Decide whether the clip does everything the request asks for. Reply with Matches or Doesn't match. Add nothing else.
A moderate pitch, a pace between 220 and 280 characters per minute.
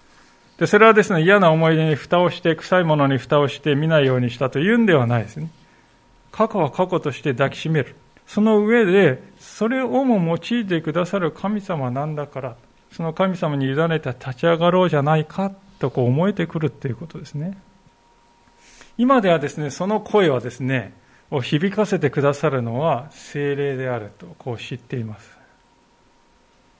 Doesn't match